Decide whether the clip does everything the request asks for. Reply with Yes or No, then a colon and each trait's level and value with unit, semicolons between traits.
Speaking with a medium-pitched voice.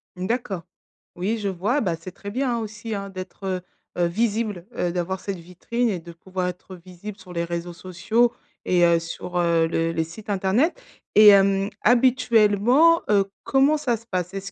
No: high, 195 Hz